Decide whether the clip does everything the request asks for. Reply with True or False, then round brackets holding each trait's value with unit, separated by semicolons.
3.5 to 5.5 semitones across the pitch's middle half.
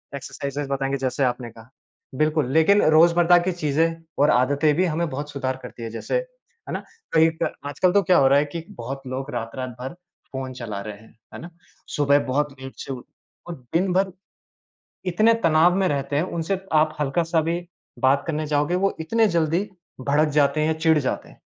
True (3.8 semitones)